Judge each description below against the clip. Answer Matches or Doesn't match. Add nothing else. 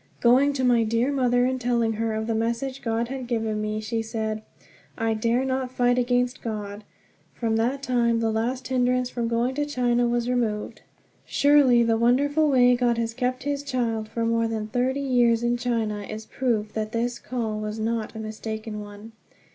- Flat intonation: Matches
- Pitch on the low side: Doesn't match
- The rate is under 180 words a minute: Doesn't match